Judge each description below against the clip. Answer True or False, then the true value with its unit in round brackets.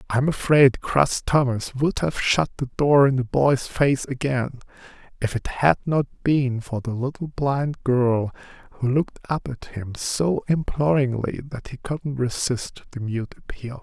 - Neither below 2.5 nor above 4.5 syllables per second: True (4.0 syllables/s)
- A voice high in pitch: False (135 Hz)